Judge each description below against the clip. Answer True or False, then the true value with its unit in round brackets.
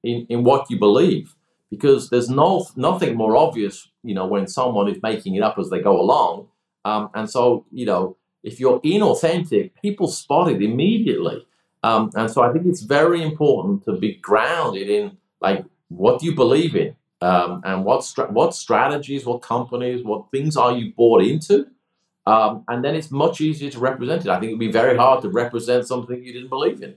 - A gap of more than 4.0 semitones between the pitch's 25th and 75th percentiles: True (4.8 semitones)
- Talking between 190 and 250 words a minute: True (200 wpm)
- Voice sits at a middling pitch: False (125 Hz)